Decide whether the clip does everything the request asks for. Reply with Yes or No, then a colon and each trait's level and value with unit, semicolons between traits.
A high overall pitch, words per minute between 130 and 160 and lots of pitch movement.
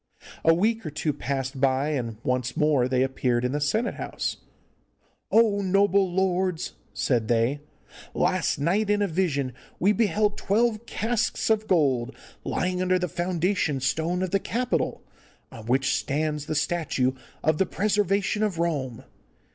No: medium, 170 Hz; average, 150 wpm; wide, 6.5 semitones